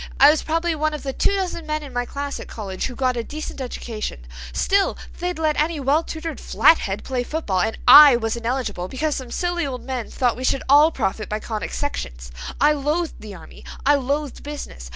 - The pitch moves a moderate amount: Yes, average, 4.9 semitones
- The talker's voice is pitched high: Yes, very high, 270 Hz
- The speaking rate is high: Yes, fast, 210 wpm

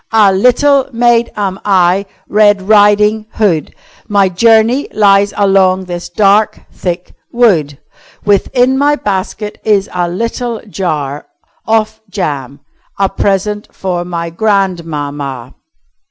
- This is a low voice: No, high, 200 Hz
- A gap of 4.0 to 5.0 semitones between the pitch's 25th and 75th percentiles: No, average, 3.5 semitones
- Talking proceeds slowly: Yes, slow, 115 wpm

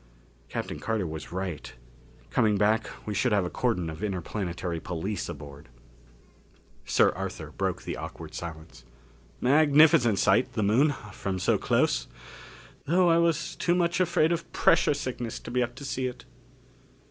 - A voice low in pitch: Yes, low, 110 Hz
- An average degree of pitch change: No, wide, 8.2 semitones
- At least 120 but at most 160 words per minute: Yes, average, 150 wpm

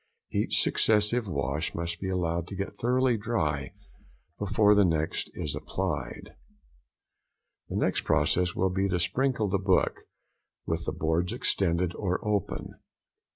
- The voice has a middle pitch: No, very low, 95 Hz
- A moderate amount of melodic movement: Yes, average, 3.7 semitones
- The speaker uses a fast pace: No, slow, 135 wpm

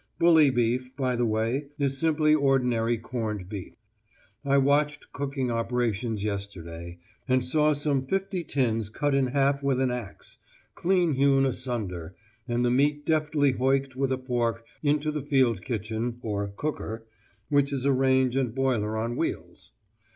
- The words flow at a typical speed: Yes, average, 150 wpm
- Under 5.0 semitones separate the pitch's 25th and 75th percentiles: Yes, average, 3.5 semitones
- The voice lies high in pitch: No, low, 130 Hz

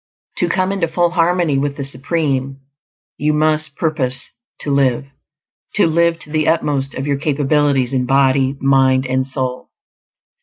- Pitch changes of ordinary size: Yes, average, 3.0 semitones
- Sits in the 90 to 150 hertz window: Yes, medium, 140 Hz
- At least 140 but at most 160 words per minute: Yes, average, 150 wpm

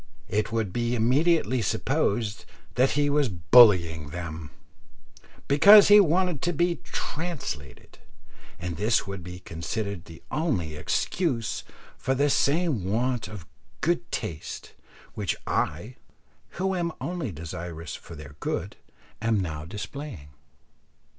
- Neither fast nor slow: No, slow, 120 wpm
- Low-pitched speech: Yes, low, 110 Hz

